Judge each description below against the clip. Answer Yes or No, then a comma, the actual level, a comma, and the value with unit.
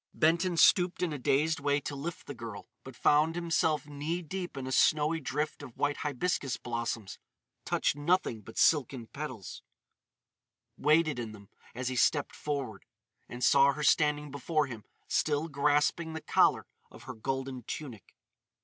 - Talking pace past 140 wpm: Yes, average, 150 wpm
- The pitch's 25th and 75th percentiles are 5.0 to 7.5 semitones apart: No, average, 3.5 semitones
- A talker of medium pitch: Yes, medium, 145 Hz